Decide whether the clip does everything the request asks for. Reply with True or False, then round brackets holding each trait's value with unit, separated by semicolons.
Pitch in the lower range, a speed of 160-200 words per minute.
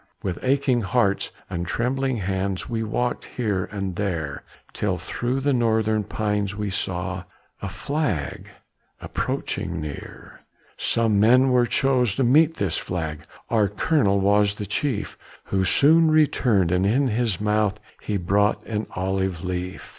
False (105 Hz; 140 wpm)